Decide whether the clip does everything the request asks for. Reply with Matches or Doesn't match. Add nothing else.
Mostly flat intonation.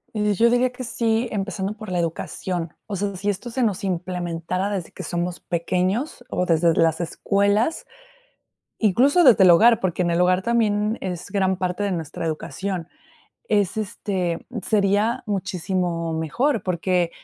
Doesn't match